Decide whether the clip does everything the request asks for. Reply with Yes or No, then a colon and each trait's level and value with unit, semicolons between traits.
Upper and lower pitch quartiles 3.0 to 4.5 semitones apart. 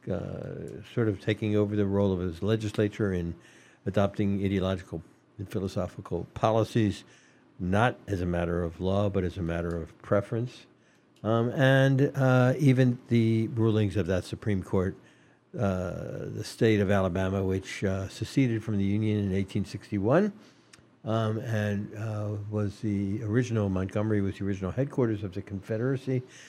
No: narrow, 2.5 semitones